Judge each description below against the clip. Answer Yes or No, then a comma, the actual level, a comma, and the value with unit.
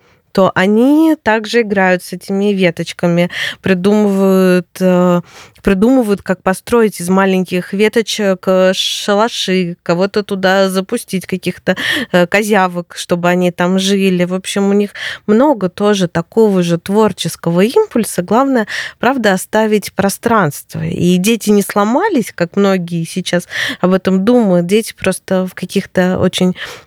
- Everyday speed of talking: Yes, average, 120 wpm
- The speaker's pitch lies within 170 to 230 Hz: Yes, high, 190 Hz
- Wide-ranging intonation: No, average, 2.9 semitones